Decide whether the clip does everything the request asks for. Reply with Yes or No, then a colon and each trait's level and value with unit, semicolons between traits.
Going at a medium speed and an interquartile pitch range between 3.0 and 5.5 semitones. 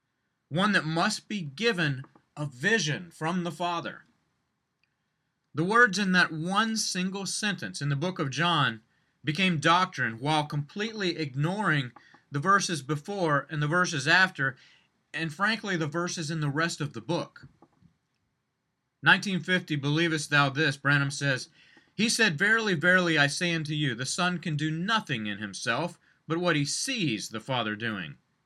Yes: average, 150 wpm; average, 4.0 semitones